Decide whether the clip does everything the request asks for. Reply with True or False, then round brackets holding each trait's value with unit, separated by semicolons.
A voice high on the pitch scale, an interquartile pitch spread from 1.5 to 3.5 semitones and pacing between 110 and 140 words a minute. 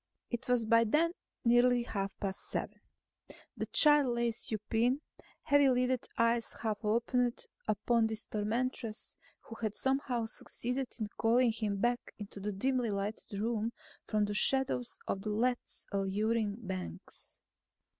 True (230 Hz; 2.8 semitones; 135 wpm)